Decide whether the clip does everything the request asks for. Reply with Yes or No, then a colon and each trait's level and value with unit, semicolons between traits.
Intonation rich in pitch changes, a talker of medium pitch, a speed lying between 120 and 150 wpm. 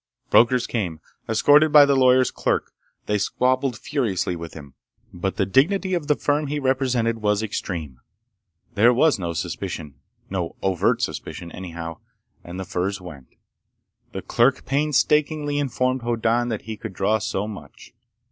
No: wide, 6.4 semitones; low, 115 Hz; average, 140 wpm